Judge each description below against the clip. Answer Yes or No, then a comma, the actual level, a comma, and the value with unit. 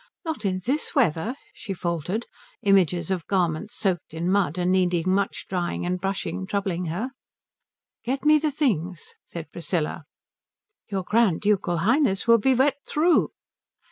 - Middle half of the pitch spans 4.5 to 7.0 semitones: Yes, average, 5.0 semitones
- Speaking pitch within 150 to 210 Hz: Yes, high, 190 Hz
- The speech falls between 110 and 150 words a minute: Yes, average, 145 wpm